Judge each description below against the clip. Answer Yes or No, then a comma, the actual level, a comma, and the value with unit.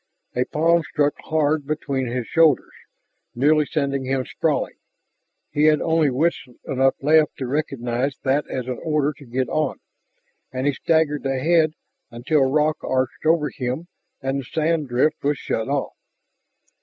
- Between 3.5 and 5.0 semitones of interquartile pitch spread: No, average, 2.9 semitones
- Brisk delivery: No, average, 150 wpm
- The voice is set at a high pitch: No, medium, 145 Hz